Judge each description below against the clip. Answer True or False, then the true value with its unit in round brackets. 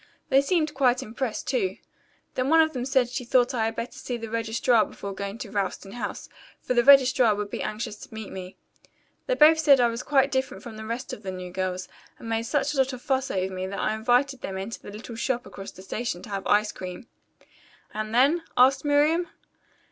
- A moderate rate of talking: False (225 wpm)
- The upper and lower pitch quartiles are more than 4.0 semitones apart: True (4.4 semitones)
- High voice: True (235 Hz)